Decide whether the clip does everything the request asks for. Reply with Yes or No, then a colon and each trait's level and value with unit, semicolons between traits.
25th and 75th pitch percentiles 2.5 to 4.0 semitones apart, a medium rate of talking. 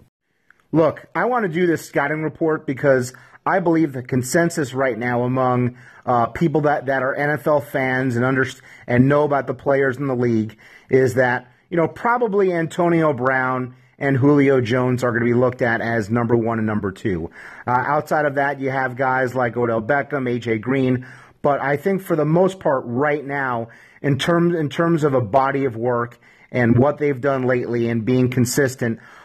Yes: average, 3.1 semitones; average, 190 wpm